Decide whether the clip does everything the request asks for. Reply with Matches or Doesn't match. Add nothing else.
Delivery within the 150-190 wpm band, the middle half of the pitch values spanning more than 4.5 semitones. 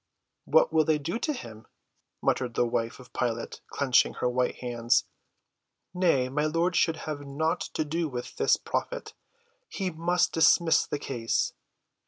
Matches